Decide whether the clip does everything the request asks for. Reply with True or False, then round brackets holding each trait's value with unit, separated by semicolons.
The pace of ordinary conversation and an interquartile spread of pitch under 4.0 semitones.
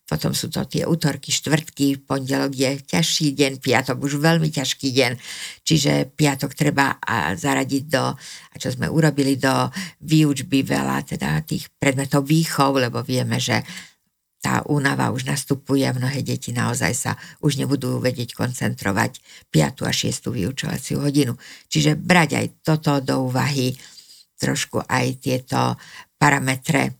True (140 wpm; 2.4 semitones)